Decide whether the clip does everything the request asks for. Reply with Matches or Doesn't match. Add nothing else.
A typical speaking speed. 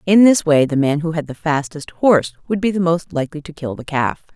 Doesn't match